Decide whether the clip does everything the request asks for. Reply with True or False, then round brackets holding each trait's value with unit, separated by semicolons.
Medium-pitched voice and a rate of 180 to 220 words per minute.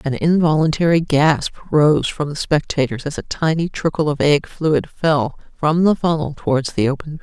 True (150 Hz; 185 wpm)